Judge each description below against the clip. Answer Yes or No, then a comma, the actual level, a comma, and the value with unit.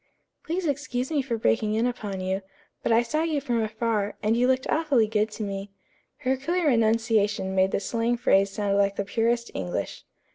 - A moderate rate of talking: Yes, average, 190 wpm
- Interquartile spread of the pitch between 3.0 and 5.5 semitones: Yes, average, 3.9 semitones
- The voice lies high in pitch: Yes, high, 230 Hz